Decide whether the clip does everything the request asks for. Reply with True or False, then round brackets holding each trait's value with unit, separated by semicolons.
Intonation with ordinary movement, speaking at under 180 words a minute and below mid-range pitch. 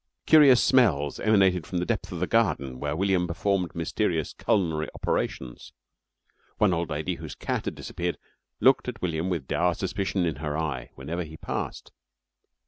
True (4.0 semitones; 160 wpm; 90 Hz)